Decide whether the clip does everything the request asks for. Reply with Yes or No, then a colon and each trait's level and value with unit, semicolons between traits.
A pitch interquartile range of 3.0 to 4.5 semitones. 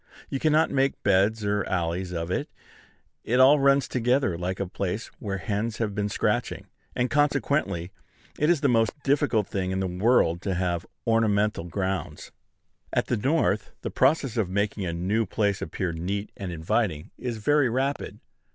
No: average, 5.3 semitones